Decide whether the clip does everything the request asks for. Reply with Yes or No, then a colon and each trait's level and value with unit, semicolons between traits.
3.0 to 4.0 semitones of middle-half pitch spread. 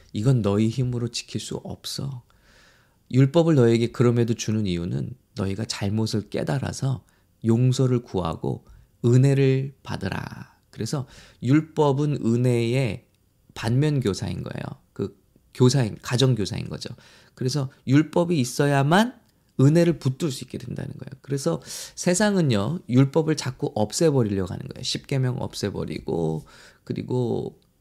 No: average, 4.4 semitones